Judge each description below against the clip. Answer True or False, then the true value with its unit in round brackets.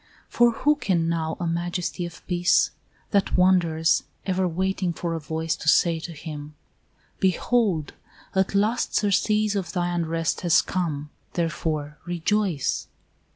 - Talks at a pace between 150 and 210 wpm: False (135 wpm)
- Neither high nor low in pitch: True (175 Hz)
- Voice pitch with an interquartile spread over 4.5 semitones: False (2.8 semitones)